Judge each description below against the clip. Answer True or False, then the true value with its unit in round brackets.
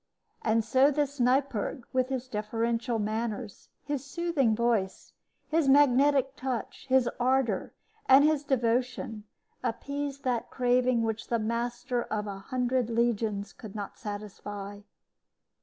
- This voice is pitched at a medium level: False (240 Hz)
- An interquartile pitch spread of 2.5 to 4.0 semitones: True (3.3 semitones)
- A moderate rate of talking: False (125 wpm)